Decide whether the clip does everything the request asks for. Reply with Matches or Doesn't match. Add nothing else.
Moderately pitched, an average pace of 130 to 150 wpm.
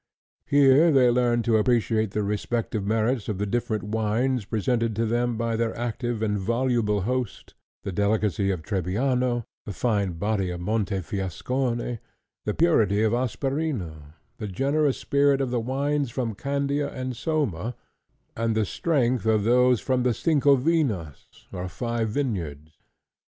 Doesn't match